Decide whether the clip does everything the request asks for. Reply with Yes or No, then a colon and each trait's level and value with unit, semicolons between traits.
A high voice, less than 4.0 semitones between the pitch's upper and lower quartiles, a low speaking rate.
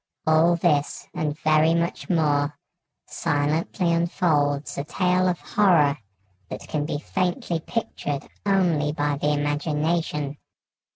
No: medium, 155 Hz; average, 2.7 semitones; slow, 115 wpm